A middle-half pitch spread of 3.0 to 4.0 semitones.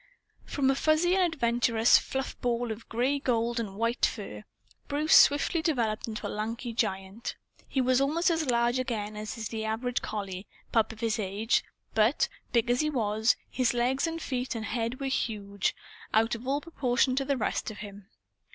Yes: average, 3.5 semitones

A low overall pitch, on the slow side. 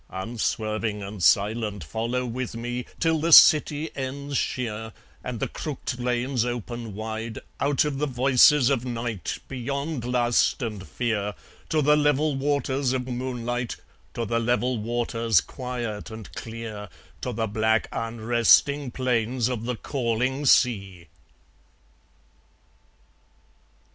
Yes: low, 120 Hz; slow, 125 wpm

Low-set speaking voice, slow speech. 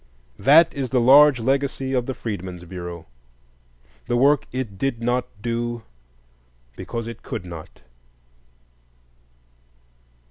Yes: low, 120 Hz; slow, 110 wpm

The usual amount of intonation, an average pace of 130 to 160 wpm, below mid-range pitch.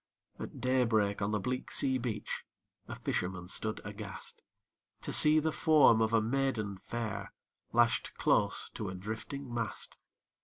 Yes: average, 3.9 semitones; average, 150 wpm; low, 110 Hz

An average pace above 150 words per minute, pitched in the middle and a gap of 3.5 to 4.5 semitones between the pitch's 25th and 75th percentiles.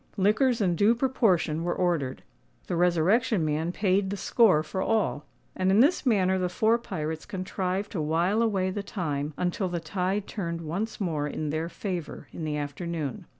Yes: average, 175 wpm; medium, 180 Hz; average, 4.1 semitones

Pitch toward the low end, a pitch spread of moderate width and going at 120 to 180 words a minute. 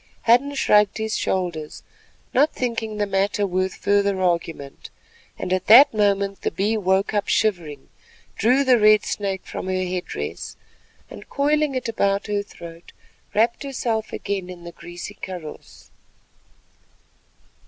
No: high, 200 Hz; average, 3.2 semitones; average, 140 wpm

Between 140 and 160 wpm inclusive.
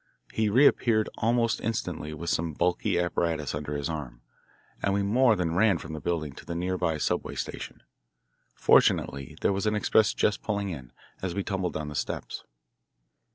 No: average, 175 wpm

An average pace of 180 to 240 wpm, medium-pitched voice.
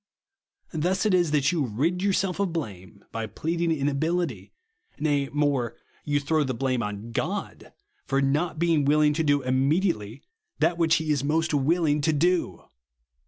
No: average, 160 wpm; medium, 150 Hz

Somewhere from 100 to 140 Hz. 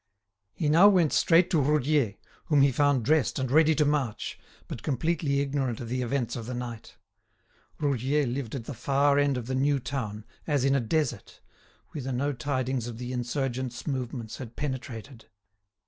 Yes: low, 135 Hz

